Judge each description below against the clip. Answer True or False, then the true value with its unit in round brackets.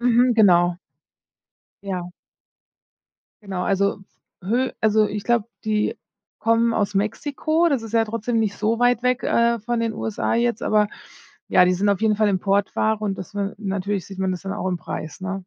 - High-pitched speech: True (210 Hz)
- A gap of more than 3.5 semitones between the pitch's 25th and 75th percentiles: False (3.0 semitones)